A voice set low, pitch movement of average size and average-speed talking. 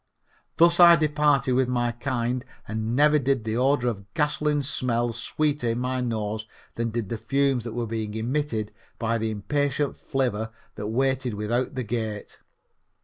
Yes: low, 120 Hz; average, 3.8 semitones; average, 160 wpm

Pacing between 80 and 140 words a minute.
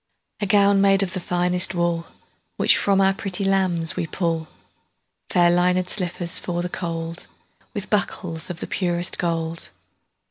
Yes: slow, 135 wpm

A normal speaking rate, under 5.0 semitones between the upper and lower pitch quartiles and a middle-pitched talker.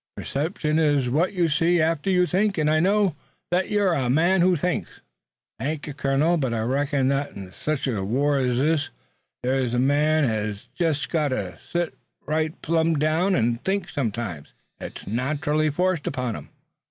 Yes: average, 170 wpm; average, 4.4 semitones; medium, 150 Hz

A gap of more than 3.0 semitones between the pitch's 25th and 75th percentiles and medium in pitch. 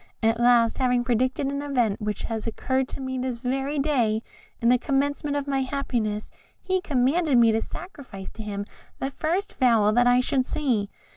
No: average, 3.5 semitones; very high, 255 Hz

